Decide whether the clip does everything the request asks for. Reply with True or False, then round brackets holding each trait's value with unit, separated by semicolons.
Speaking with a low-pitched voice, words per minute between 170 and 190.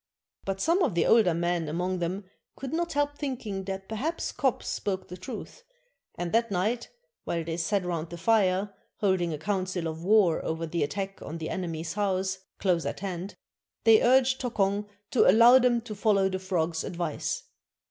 False (190 Hz; 180 wpm)